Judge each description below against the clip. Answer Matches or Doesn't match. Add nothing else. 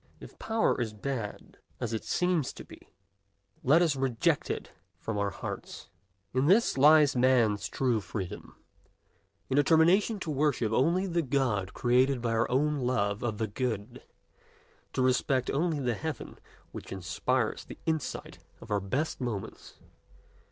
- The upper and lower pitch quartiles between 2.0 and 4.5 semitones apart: Doesn't match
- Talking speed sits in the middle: Matches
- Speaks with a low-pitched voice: Matches